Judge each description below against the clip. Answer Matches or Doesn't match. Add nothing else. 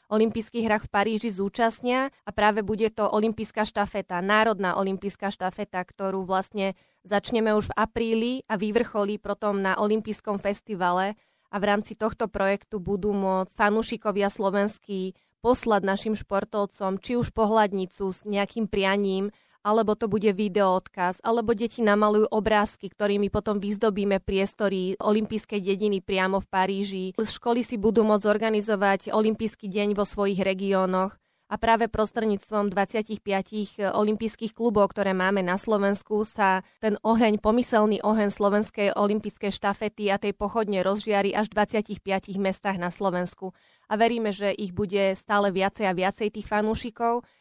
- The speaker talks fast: Doesn't match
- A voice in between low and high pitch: Doesn't match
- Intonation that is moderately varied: Doesn't match